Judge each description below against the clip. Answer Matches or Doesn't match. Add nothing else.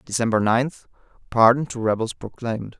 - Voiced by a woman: Doesn't match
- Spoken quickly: Doesn't match